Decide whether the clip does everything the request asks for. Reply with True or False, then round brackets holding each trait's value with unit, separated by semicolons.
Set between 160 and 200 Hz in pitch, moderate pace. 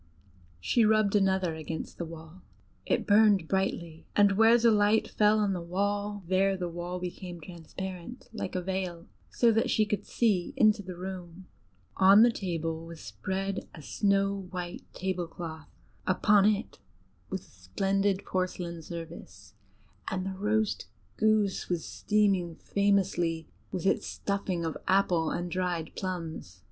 True (185 Hz; 145 wpm)